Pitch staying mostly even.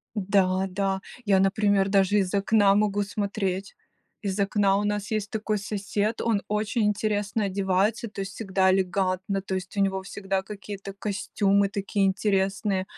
Yes: narrow, 1.2 semitones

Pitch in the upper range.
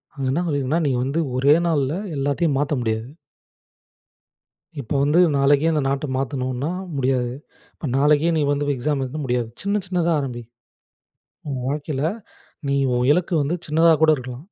No: medium, 140 Hz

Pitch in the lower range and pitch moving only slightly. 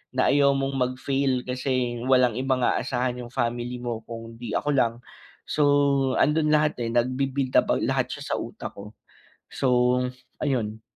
Yes: low, 130 Hz; narrow, 2.2 semitones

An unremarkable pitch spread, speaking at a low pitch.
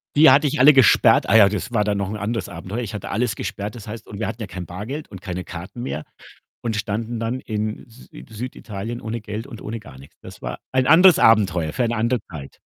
Yes: average, 3.2 semitones; low, 110 Hz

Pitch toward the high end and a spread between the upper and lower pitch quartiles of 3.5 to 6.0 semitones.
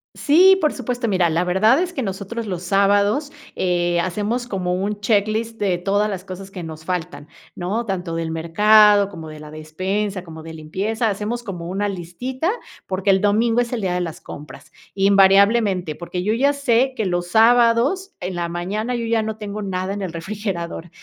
Yes: high, 200 Hz; average, 4.1 semitones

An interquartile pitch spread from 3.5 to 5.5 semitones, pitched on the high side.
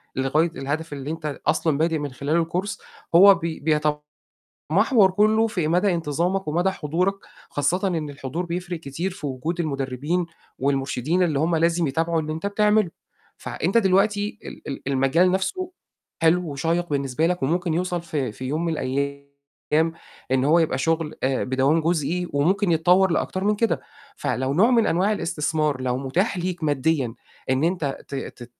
No: average, 4.2 semitones; medium, 160 Hz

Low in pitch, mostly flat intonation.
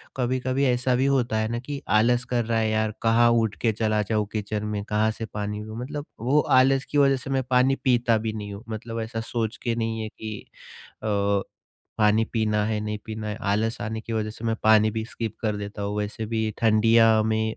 Yes: low, 110 Hz; narrow, 1.7 semitones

